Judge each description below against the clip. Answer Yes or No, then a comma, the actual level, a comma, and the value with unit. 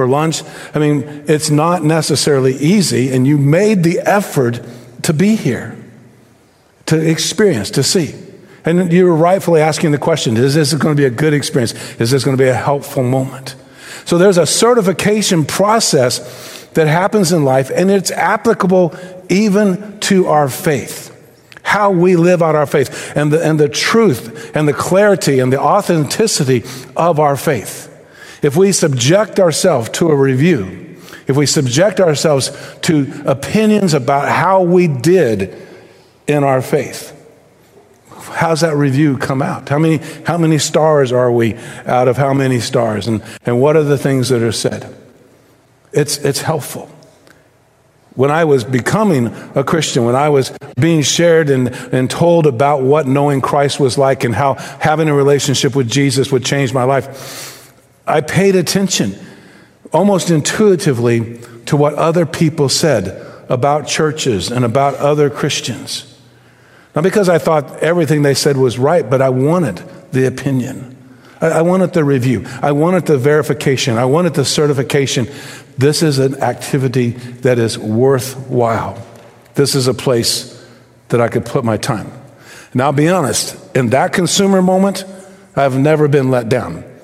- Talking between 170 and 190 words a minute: No, average, 160 wpm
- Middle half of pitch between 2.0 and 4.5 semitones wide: Yes, average, 4.2 semitones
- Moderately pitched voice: Yes, medium, 145 Hz